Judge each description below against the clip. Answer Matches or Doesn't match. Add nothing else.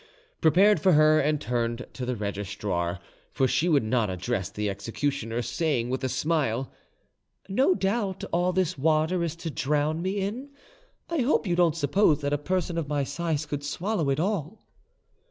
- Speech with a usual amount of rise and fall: Doesn't match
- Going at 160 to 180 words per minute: Matches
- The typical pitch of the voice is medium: Matches